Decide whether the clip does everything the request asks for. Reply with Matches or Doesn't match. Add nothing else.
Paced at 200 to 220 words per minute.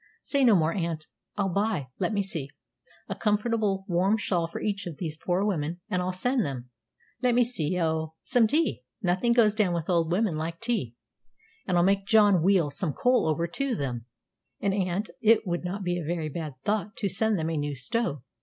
Matches